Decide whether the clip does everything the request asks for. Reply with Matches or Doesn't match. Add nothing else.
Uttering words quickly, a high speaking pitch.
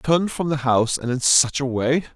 Doesn't match